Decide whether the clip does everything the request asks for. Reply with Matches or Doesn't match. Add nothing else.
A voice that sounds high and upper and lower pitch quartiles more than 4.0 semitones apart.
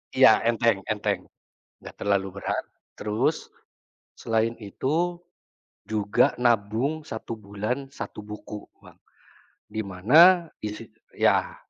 Doesn't match